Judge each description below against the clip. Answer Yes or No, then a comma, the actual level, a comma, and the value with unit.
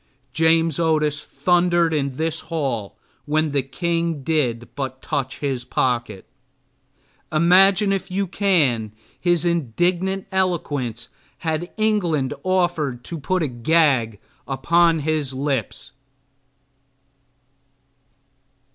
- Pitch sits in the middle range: Yes, medium, 155 Hz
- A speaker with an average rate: No, slow, 100 wpm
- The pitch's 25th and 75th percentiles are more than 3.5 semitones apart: Yes, average, 4.6 semitones